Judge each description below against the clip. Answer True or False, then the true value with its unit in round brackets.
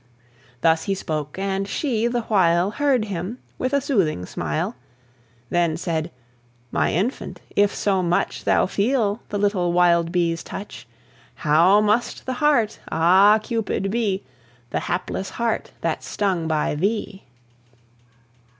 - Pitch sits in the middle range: False (195 Hz)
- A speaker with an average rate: False (130 wpm)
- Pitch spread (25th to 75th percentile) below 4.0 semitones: False (4.3 semitones)